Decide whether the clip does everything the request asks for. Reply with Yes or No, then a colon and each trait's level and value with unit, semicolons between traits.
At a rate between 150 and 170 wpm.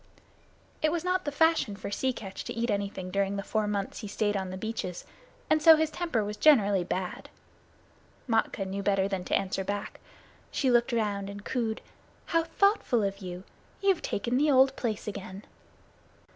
No: average, 180 wpm